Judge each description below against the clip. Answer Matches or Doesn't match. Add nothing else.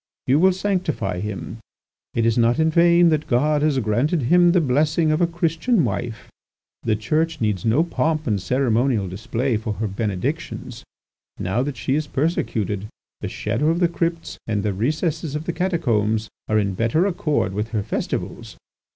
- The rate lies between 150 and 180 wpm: Matches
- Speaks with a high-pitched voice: Doesn't match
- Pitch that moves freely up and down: Matches